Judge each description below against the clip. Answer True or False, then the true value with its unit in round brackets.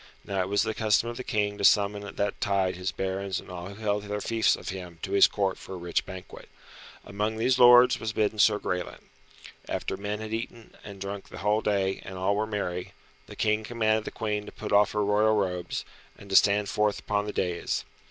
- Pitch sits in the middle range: False (105 Hz)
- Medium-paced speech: False (225 wpm)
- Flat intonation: True (1.9 semitones)